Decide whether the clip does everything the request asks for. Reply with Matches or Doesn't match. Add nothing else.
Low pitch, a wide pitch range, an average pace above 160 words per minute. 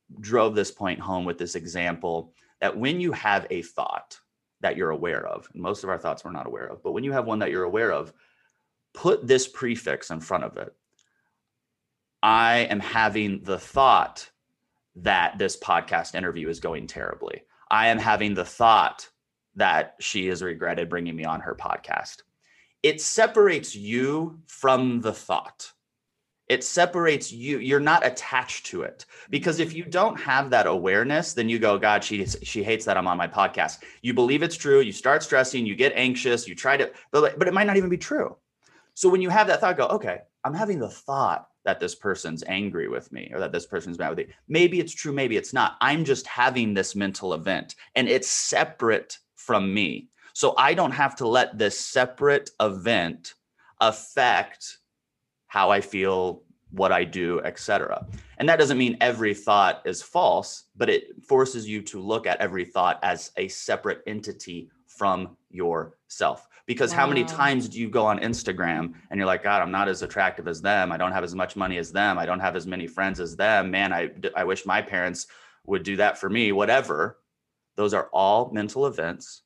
Matches